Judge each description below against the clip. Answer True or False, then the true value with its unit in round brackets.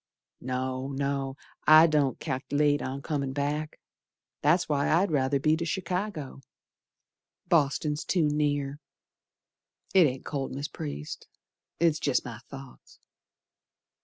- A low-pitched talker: False (145 Hz)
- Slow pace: True (115 wpm)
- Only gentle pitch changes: True (2.3 semitones)